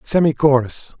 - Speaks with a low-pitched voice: No, medium, 145 Hz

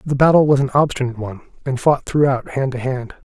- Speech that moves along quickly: Yes, fast, 220 wpm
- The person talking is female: No, male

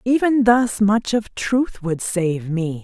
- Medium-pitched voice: No, high, 210 Hz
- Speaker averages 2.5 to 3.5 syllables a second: Yes, 3.3 syllables/s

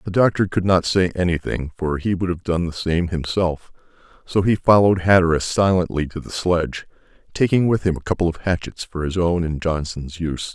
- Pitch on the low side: Yes, very low, 85 Hz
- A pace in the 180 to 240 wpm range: Yes, average, 200 wpm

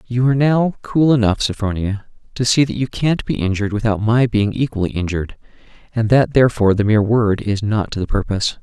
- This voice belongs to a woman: No, male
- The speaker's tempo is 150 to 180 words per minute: No, average, 200 wpm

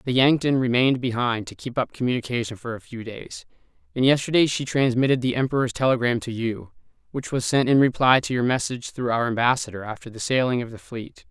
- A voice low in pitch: Yes, low, 125 Hz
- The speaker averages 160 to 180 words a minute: No, average, 200 wpm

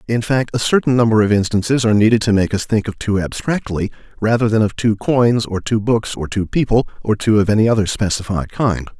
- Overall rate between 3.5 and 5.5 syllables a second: No, 5.8 syllables/s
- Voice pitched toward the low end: Yes, low, 110 Hz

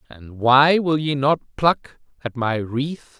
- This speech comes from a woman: No, male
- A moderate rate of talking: Yes, average, 170 wpm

